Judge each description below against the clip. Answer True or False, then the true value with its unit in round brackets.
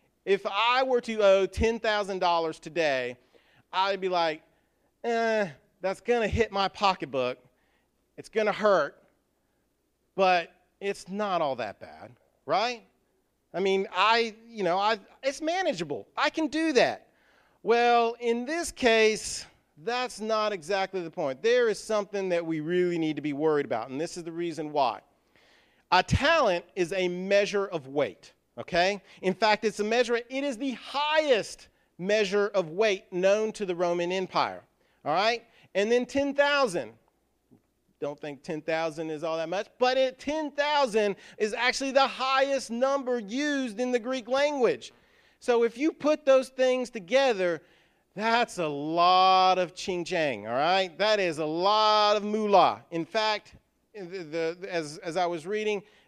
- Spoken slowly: False (155 wpm)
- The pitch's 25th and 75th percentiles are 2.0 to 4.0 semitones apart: False (5.4 semitones)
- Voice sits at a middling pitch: False (205 Hz)